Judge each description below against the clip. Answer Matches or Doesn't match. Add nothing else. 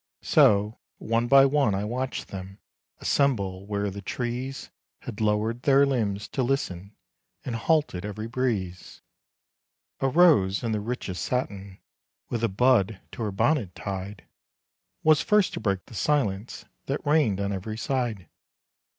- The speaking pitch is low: Matches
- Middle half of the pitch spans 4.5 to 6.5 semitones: Matches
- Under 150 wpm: Matches